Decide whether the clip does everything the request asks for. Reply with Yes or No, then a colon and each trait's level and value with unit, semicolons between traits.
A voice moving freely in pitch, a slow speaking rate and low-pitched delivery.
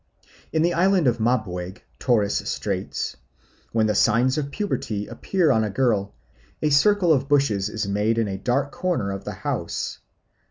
No: wide, 6.0 semitones; average, 165 wpm; low, 120 Hz